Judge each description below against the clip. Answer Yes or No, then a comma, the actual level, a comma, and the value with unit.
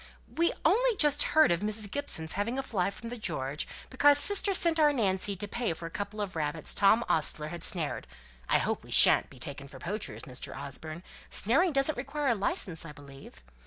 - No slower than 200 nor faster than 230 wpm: Yes, fast, 205 wpm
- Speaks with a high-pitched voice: Yes, high, 205 Hz